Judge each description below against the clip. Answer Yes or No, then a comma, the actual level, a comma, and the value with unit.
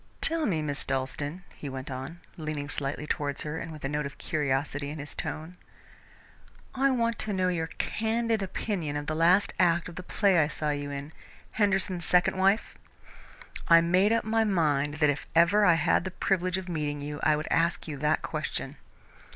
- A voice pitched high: No, medium, 165 Hz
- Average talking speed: Yes, average, 190 wpm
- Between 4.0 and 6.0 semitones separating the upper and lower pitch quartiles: Yes, average, 4.3 semitones